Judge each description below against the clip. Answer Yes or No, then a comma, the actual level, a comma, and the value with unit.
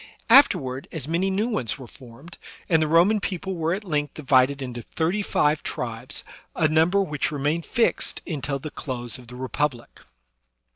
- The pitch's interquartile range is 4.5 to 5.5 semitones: Yes, average, 5.0 semitones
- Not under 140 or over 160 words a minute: No, average, 175 wpm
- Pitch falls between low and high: Yes, medium, 150 Hz